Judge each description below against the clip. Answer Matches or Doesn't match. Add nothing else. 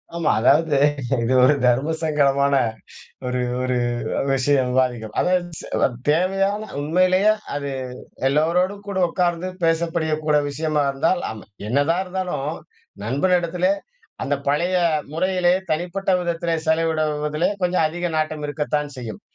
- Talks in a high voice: Doesn't match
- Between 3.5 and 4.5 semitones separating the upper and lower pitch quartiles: Matches